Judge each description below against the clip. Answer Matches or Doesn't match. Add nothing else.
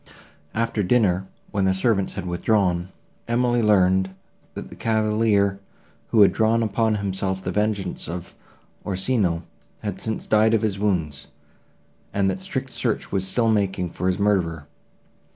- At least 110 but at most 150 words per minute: Matches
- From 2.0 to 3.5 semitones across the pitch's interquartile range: Matches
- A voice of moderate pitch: Doesn't match